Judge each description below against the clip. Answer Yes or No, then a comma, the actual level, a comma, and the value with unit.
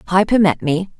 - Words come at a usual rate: Yes, average, 180 wpm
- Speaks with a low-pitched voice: No, medium, 185 Hz